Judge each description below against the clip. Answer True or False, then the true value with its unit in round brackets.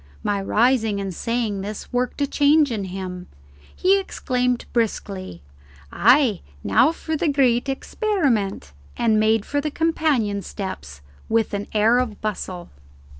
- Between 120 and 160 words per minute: True (135 wpm)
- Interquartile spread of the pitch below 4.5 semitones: False (5.5 semitones)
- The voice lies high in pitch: True (225 Hz)